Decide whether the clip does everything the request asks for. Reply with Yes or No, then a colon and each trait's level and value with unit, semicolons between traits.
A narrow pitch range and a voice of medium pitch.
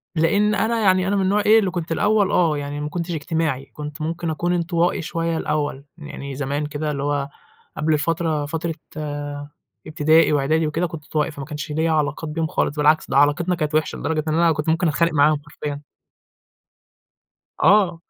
Yes: narrow, 2.3 semitones; medium, 160 Hz